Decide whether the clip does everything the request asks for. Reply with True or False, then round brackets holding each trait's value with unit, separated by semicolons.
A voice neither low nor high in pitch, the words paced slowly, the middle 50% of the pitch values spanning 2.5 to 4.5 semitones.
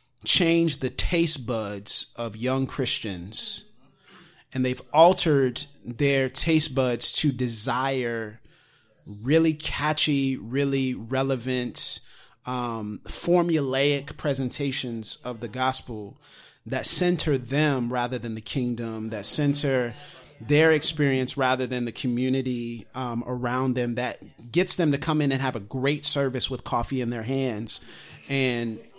False (130 Hz; 125 wpm; 2.9 semitones)